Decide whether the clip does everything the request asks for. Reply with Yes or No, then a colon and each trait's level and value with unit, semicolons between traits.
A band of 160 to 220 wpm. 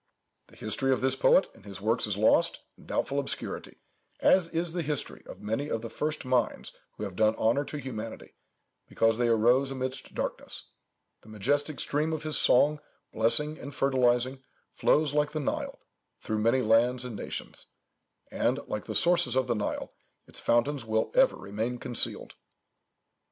Yes: average, 165 wpm